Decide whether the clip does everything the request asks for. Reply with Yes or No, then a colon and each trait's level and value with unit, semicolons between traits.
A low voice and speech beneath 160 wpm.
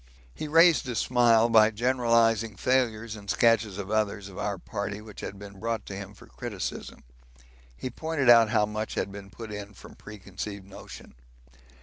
No: low, 110 Hz; average, 170 wpm